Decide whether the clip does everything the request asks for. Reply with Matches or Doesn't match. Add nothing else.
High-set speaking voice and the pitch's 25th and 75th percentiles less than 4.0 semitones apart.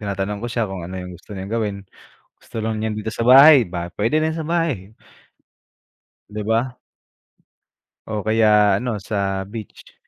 Doesn't match